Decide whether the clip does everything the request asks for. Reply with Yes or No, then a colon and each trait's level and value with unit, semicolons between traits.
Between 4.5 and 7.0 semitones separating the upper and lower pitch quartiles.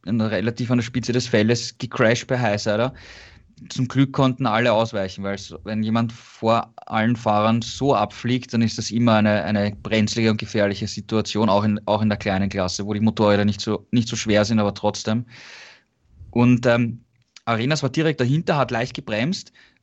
No: narrow, 2.5 semitones